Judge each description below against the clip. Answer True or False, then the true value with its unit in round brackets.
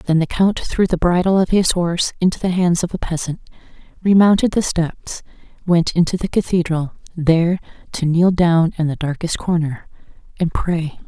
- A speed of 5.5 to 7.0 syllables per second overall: False (5.0 syllables/s)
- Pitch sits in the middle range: True (170 Hz)